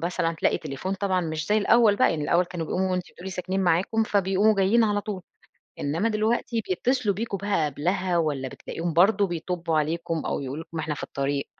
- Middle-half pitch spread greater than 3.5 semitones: Yes, average, 3.9 semitones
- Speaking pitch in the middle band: Yes, medium, 180 Hz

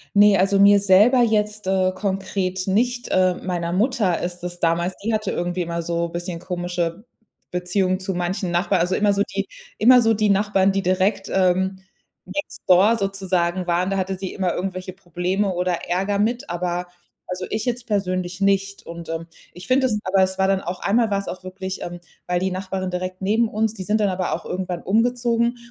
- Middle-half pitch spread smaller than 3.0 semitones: Yes, narrow, 2.4 semitones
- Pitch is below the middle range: No, high, 190 Hz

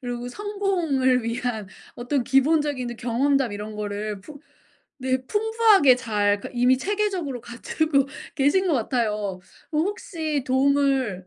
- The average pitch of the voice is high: Yes, very high, 260 Hz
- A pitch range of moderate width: Yes, average, 4.6 semitones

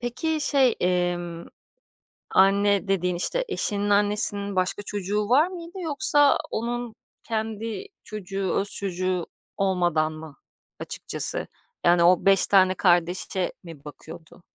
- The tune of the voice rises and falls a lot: No, average, 3.9 semitones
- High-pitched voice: Yes, high, 195 Hz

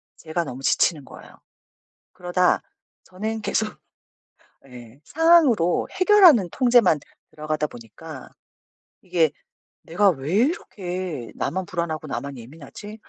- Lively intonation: Yes, wide, 5.9 semitones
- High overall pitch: No, medium, 175 Hz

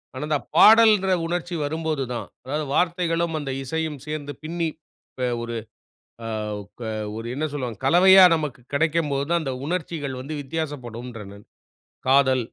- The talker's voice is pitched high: No, medium, 150 Hz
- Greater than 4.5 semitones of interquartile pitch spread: No, average, 4.1 semitones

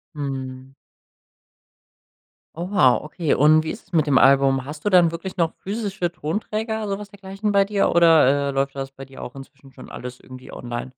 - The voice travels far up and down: Yes, wide, 6.2 semitones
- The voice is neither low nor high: Yes, medium, 155 Hz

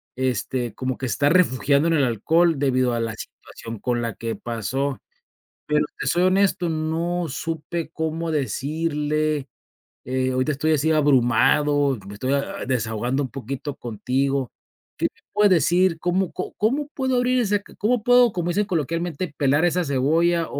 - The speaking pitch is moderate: Yes, medium, 150 Hz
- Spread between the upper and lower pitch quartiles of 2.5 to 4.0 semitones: No, average, 4.8 semitones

